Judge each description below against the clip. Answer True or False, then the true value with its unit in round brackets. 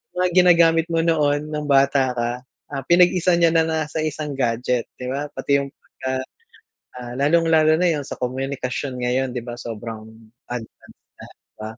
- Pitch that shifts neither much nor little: True (4.4 semitones)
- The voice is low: False (145 Hz)